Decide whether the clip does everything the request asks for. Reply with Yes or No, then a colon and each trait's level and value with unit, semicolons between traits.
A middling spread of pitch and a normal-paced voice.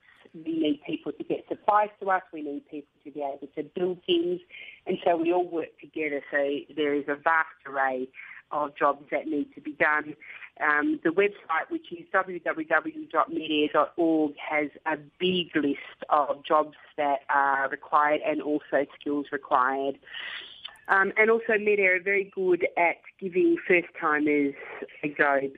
Yes: average, 4.2 semitones; average, 155 wpm